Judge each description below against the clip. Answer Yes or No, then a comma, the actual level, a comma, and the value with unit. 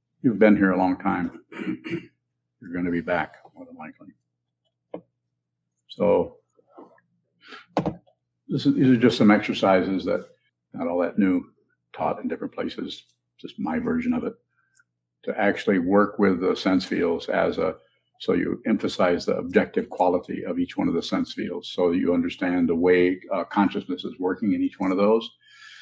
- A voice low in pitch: Yes, very low, 95 Hz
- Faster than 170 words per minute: No, average, 165 wpm